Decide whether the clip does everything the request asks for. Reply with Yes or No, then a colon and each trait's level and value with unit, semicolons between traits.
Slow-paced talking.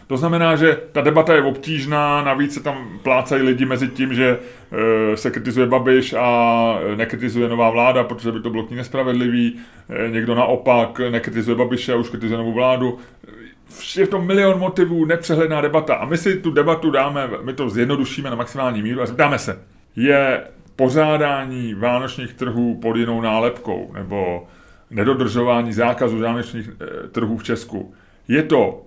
No: average, 155 wpm